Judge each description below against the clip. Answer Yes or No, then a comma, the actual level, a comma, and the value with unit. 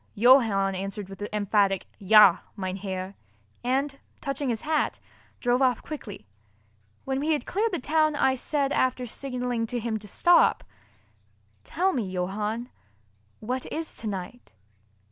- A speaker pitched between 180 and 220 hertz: No, high, 240 Hz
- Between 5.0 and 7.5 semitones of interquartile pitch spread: Yes, wide, 5.4 semitones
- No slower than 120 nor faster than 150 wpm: Yes, average, 140 wpm